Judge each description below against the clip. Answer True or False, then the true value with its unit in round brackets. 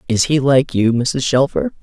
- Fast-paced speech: False (195 wpm)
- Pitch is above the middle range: False (130 Hz)